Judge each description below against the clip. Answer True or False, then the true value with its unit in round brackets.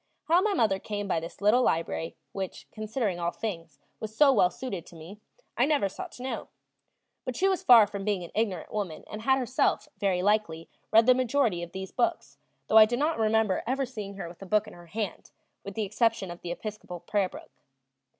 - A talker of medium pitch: False (210 Hz)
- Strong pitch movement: False (4.5 semitones)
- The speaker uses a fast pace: True (215 wpm)